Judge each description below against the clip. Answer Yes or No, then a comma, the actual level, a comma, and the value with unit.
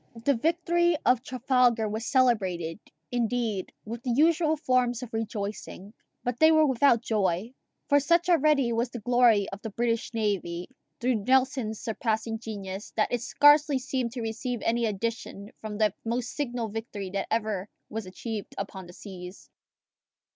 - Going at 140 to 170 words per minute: Yes, average, 155 wpm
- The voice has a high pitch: Yes, high, 230 Hz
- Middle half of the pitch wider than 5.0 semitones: No, average, 3.4 semitones